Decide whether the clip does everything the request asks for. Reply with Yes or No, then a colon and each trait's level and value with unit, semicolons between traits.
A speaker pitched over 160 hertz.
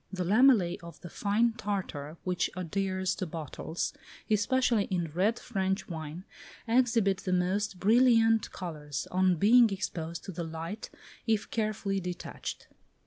Yes: high, 190 Hz